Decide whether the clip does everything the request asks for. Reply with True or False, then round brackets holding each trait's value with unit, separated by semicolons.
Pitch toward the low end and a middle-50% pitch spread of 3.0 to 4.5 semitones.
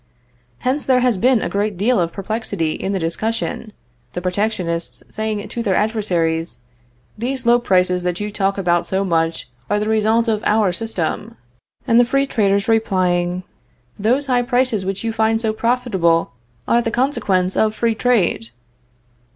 False (215 Hz; 4.1 semitones)